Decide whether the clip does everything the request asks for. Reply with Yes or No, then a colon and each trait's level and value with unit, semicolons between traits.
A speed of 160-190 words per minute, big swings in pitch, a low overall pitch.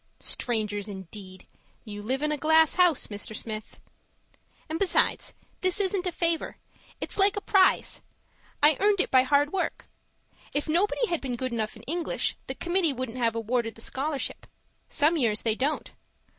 No: average, 165 wpm; wide, 7.2 semitones; very high, 285 Hz